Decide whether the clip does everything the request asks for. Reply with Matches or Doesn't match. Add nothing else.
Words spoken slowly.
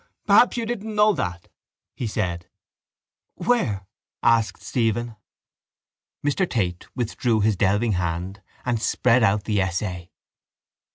Matches